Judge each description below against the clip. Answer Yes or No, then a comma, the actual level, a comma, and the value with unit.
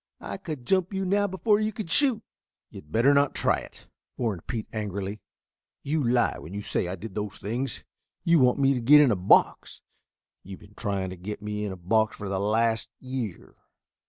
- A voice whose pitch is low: Yes, low, 115 Hz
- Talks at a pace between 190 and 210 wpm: Yes, average, 200 wpm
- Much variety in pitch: Yes, wide, 6.3 semitones